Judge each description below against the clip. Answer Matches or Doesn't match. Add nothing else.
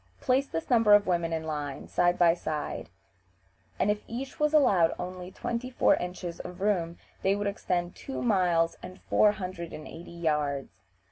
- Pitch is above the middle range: Doesn't match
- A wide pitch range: Doesn't match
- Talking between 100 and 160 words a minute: Doesn't match